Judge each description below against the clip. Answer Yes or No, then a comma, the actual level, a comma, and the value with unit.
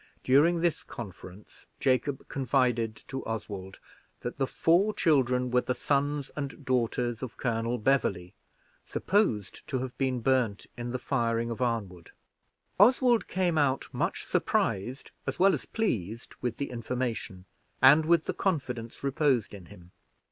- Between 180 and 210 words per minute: No, average, 140 wpm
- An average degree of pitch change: Yes, average, 3.8 semitones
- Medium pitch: No, low, 125 Hz